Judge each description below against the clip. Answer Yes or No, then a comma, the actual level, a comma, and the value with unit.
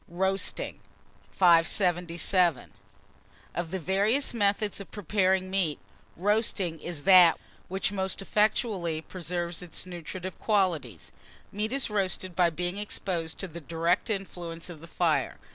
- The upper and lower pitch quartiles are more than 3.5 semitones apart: No, narrow, 2.6 semitones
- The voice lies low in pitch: No, medium, 185 Hz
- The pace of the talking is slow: Yes, slow, 125 wpm